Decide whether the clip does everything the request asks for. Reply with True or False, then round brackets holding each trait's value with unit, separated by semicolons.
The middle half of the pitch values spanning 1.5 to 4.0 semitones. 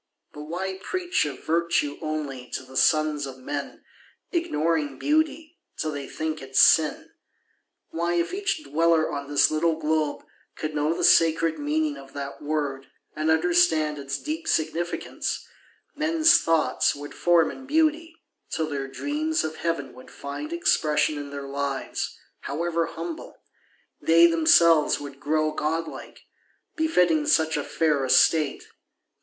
True (2.9 semitones)